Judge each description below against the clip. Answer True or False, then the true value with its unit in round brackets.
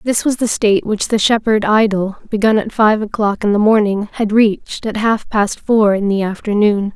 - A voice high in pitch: True (210 Hz)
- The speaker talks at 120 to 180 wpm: False (205 wpm)